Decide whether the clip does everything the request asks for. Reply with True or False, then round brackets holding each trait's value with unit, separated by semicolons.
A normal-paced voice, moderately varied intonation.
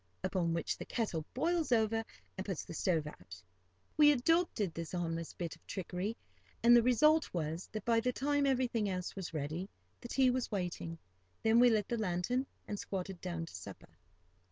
False (180 wpm; 6.2 semitones)